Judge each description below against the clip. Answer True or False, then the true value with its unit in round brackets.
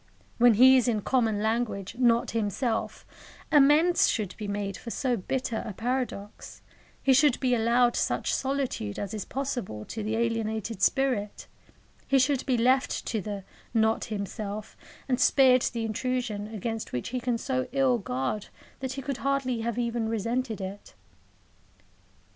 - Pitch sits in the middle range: False (235 Hz)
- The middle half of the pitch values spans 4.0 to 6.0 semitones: False (3.3 semitones)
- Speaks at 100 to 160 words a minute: True (155 wpm)